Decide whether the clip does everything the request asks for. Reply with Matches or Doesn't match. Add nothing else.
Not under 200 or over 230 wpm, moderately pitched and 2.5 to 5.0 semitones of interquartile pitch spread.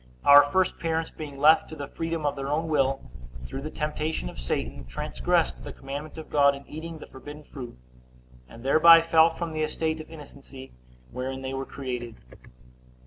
Doesn't match